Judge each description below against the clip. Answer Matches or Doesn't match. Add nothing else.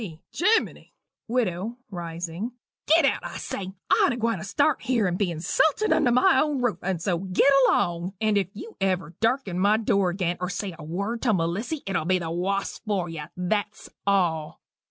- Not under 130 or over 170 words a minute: Doesn't match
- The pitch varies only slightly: Doesn't match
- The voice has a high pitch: Matches